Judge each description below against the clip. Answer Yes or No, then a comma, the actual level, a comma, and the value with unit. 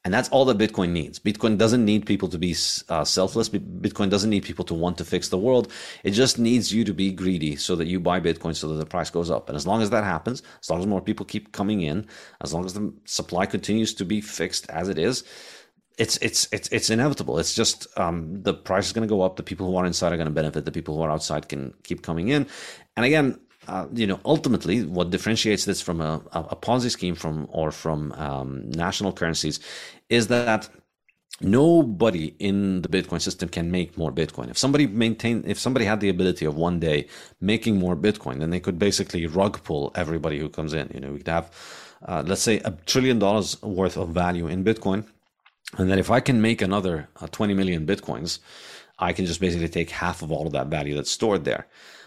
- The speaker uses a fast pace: Yes, fast, 230 wpm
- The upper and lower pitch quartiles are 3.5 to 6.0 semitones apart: Yes, average, 4.2 semitones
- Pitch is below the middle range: Yes, very low, 95 Hz